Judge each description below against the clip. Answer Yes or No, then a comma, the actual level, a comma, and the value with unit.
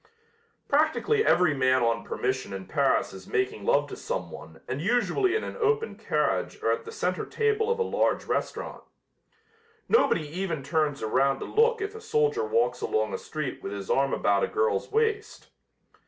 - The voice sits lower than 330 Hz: No, very high, 395 Hz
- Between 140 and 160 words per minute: No, average, 175 wpm